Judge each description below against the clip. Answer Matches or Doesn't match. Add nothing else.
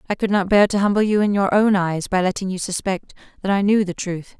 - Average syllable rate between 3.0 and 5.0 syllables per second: Doesn't match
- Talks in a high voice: Matches